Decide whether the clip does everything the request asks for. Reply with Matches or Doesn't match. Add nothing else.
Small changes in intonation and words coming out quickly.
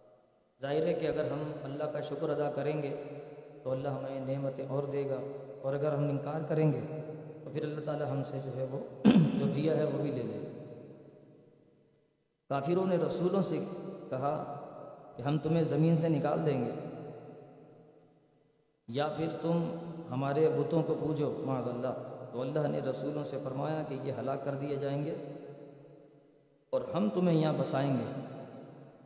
Doesn't match